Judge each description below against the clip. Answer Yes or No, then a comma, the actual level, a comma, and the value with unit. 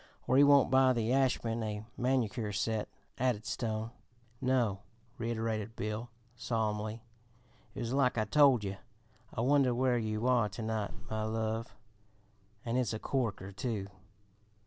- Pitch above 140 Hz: No, low, 115 Hz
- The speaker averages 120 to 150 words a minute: Yes, average, 145 wpm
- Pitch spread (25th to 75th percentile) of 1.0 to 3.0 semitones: Yes, average, 2.7 semitones